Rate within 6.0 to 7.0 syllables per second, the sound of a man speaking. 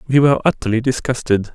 Yes: 6.7 syllables/s; male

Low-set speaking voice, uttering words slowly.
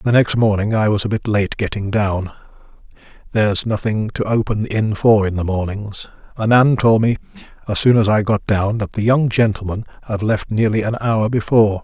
No: low, 105 Hz; average, 195 wpm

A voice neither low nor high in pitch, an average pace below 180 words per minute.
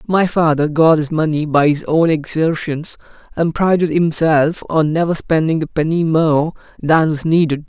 Yes: medium, 160 Hz; average, 165 wpm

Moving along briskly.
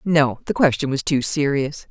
No: average, 155 wpm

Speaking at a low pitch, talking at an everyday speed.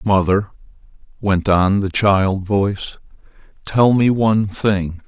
No: low, 100 Hz; slow, 120 wpm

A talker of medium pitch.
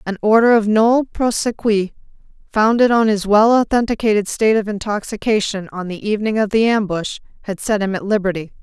No: high, 210 Hz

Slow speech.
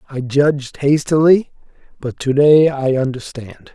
Yes: slow, 130 wpm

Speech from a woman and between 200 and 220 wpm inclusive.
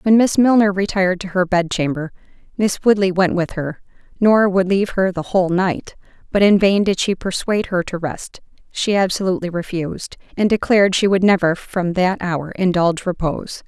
No: female; average, 175 wpm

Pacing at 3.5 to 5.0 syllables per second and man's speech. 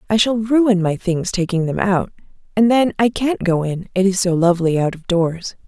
No: 4.9 syllables/s; female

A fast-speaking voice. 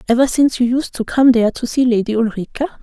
Yes: fast, 235 wpm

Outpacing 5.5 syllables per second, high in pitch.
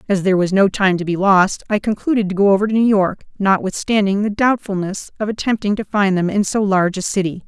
Yes: 6.0 syllables/s; high, 200 Hz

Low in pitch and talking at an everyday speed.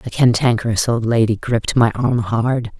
Yes: low, 115 Hz; average, 170 wpm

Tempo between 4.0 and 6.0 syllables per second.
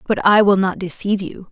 Yes: 5.9 syllables/s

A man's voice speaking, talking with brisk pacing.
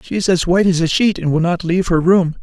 Yes: male; fast, 320 wpm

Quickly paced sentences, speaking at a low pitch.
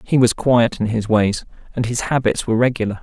Yes: fast, 220 wpm; low, 115 Hz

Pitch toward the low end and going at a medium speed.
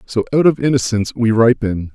Yes: low, 115 Hz; average, 185 wpm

